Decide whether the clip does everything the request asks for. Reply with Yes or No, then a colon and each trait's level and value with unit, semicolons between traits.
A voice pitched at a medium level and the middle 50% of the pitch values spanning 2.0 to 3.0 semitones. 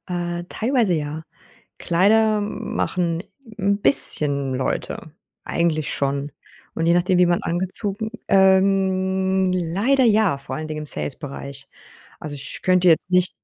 No: medium, 180 Hz; average, 3.7 semitones